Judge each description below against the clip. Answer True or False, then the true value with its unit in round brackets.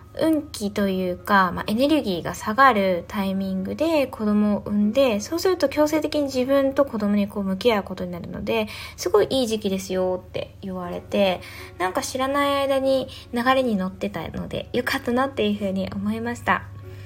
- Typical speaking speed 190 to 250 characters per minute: False (380 characters per minute)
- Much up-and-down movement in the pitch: True (6.1 semitones)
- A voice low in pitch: False (215 Hz)